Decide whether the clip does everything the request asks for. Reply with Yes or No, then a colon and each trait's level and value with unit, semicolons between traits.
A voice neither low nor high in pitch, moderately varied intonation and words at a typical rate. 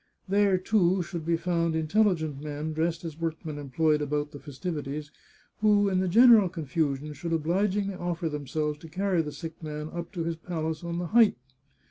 Yes: medium, 165 Hz; average, 3.2 semitones; average, 175 wpm